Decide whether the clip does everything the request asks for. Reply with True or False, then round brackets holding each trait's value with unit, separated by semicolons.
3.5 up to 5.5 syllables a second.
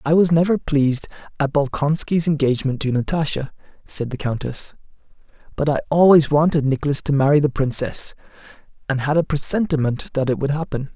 False (5.7 syllables/s)